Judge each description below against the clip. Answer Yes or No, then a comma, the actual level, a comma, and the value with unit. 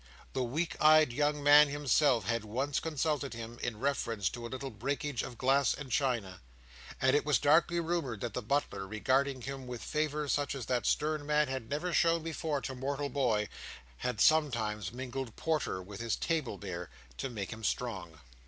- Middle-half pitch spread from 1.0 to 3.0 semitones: No, average, 4.1 semitones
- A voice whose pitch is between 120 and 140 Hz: Yes, low, 135 Hz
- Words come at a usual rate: Yes, average, 180 wpm